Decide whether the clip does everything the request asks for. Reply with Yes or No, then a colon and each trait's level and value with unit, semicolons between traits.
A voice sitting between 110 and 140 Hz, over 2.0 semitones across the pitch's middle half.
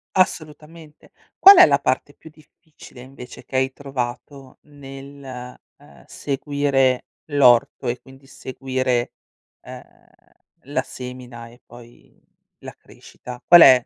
Yes: low, 135 Hz; narrow, 2.4 semitones